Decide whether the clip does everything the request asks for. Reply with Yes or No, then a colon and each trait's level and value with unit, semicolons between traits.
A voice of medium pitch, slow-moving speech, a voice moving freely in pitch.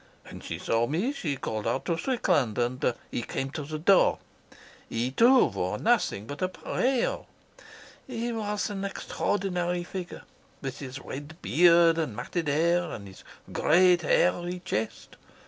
No: medium, 170 Hz; average, 145 wpm; wide, 6.1 semitones